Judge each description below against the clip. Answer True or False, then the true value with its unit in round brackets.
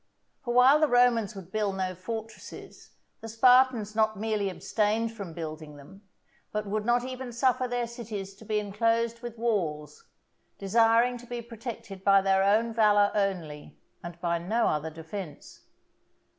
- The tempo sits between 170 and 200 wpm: False (155 wpm)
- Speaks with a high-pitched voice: True (215 Hz)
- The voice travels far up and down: False (3.4 semitones)